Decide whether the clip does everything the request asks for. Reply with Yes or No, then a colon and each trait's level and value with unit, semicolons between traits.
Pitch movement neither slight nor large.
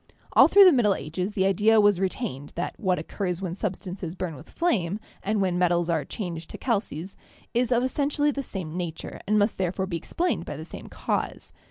Yes: average, 4.1 semitones